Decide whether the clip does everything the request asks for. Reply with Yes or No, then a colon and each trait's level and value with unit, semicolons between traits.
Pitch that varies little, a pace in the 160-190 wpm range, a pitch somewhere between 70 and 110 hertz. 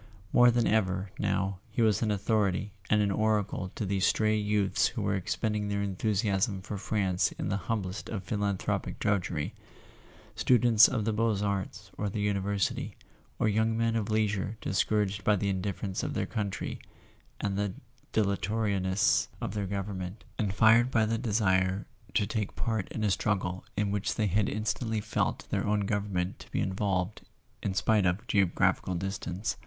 Yes: narrow, 2.0 semitones; average, 170 wpm; low, 105 Hz